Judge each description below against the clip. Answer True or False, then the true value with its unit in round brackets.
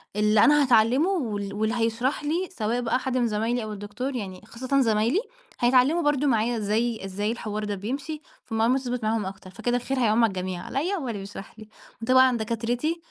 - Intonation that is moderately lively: True (3.4 semitones)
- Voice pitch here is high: True (235 Hz)